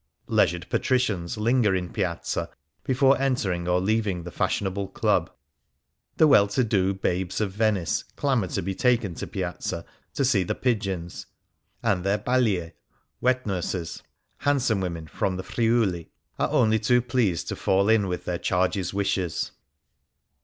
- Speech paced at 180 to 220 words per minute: No, average, 155 wpm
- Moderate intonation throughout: Yes, average, 4.5 semitones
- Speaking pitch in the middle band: No, low, 100 Hz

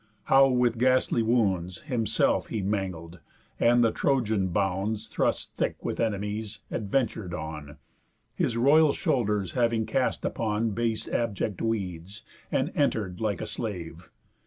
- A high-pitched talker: No, low, 110 Hz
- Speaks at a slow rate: Yes, slow, 130 wpm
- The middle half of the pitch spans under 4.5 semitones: Yes, average, 3.5 semitones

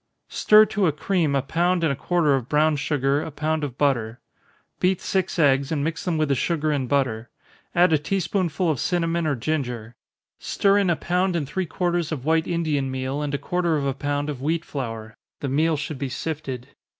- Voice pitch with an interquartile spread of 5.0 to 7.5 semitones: No, average, 3.6 semitones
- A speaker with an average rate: No, fast, 215 wpm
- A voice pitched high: No, medium, 150 Hz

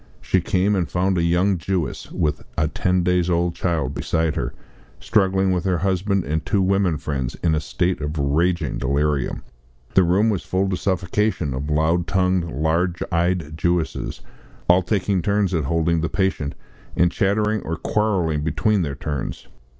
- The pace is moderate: Yes, average, 165 wpm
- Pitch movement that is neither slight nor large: Yes, average, 3.3 semitones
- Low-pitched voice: Yes, very low, 85 Hz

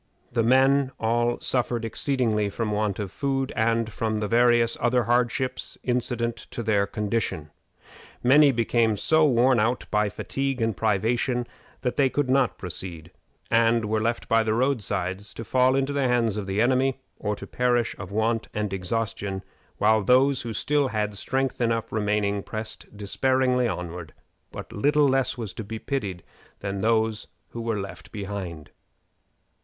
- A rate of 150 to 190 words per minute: Yes, average, 160 wpm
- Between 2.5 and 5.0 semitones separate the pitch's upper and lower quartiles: Yes, average, 3.3 semitones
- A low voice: Yes, low, 115 Hz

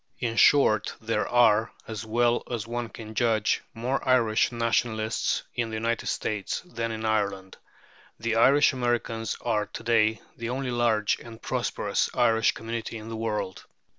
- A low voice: Yes, low, 115 Hz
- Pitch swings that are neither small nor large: No, narrow, 1.5 semitones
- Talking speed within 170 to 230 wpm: No, average, 155 wpm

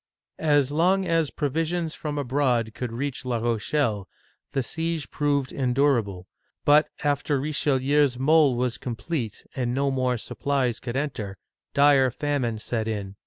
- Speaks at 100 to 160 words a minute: Yes, average, 140 wpm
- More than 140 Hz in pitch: No, low, 135 Hz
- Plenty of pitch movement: No, average, 3.5 semitones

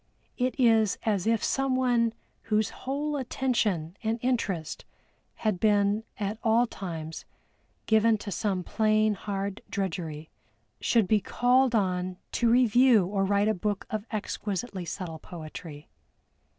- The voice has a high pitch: Yes, high, 210 Hz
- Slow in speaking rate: Yes, slow, 125 wpm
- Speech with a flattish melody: No, average, 3.6 semitones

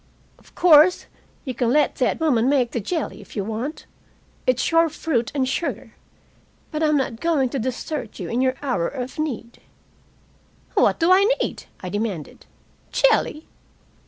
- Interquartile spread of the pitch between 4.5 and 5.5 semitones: Yes, average, 4.8 semitones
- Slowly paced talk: No, average, 160 wpm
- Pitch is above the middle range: Yes, very high, 260 Hz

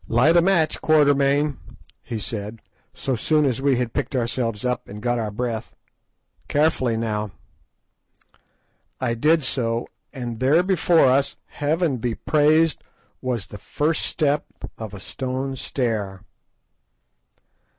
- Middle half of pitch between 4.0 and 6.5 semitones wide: Yes, average, 4.5 semitones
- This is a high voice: No, low, 130 Hz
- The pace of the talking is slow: Yes, slow, 130 wpm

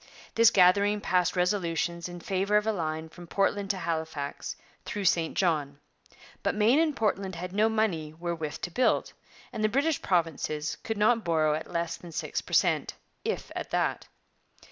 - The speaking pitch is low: No, medium, 180 Hz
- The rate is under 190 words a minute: Yes, average, 170 wpm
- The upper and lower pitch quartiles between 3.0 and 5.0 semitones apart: Yes, average, 4.2 semitones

